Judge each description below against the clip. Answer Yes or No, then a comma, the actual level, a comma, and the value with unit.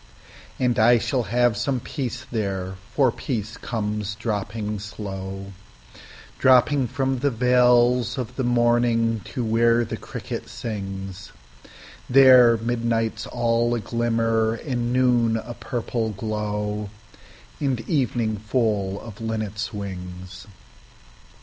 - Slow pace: Yes, slow, 105 wpm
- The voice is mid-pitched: No, low, 115 Hz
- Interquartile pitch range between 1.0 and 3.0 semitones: Yes, average, 2.7 semitones